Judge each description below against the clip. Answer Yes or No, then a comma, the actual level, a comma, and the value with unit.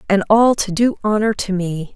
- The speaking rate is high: Yes, fast, 215 wpm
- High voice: Yes, high, 205 Hz